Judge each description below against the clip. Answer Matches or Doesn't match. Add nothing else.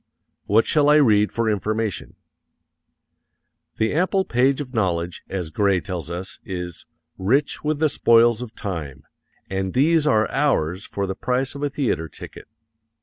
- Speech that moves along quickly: Doesn't match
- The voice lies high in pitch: Doesn't match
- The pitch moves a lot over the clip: Matches